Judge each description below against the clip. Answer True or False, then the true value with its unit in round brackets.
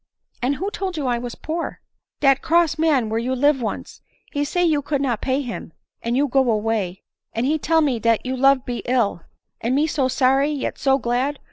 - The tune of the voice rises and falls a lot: False (3.3 semitones)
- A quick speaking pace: True (240 wpm)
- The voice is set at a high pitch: True (265 Hz)